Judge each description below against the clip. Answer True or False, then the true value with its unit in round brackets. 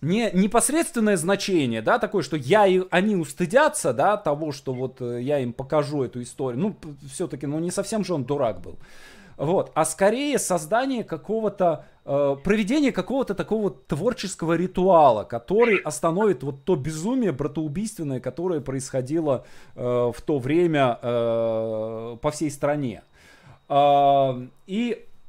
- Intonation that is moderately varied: False (6.5 semitones)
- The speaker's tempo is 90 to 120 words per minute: False (135 wpm)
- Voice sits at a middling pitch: True (165 Hz)